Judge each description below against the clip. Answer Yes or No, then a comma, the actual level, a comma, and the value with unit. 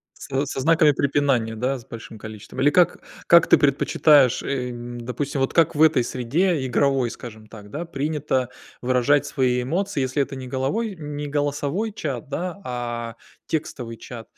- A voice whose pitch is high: No, low, 135 Hz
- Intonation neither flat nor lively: Yes, average, 3.3 semitones